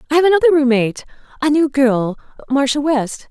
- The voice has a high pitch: Yes, very high, 275 Hz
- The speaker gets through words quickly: No, average, 165 wpm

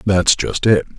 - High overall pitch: No, very low, 95 Hz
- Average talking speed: Yes, average, 185 wpm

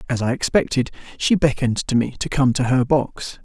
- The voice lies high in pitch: No, low, 130 Hz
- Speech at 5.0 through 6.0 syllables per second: Yes, 5.4 syllables/s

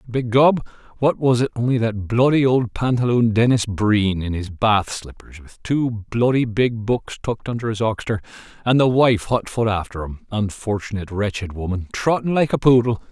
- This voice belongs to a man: Yes, male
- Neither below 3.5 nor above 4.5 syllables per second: No, 5.0 syllables/s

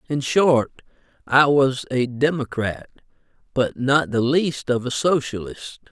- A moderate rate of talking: No, slow, 130 wpm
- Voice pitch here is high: No, low, 135 Hz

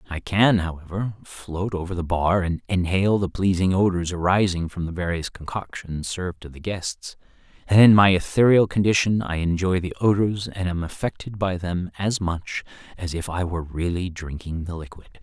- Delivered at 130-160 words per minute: No, average, 175 wpm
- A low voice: Yes, very low, 90 Hz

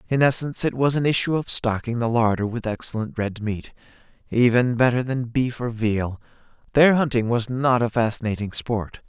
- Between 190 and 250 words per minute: No, average, 180 wpm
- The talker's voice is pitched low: Yes, low, 120 Hz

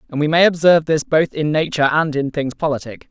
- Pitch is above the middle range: No, medium, 150 Hz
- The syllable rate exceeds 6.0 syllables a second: Yes, 6.2 syllables/s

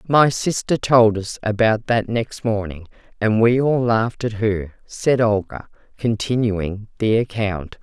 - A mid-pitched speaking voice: No, low, 110 Hz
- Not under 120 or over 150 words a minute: Yes, average, 145 wpm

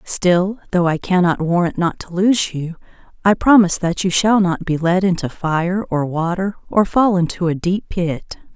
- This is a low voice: No, medium, 180 Hz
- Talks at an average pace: Yes, average, 190 wpm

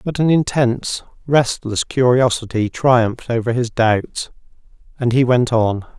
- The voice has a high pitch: No, low, 120 Hz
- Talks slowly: Yes, slow, 130 wpm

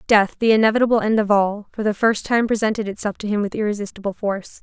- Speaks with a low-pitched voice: No, high, 210 Hz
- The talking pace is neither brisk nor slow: No, fast, 220 wpm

